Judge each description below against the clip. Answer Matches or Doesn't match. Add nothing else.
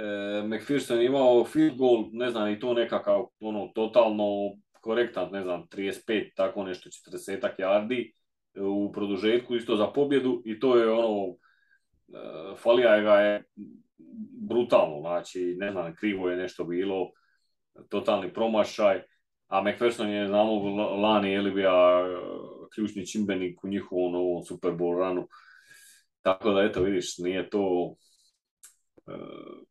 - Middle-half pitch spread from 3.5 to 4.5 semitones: Matches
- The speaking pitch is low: Matches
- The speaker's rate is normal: Matches